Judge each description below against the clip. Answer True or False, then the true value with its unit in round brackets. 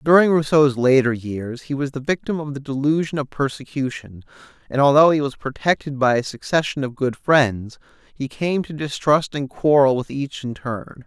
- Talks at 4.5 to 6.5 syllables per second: True (4.9 syllables/s)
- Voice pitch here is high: False (140 Hz)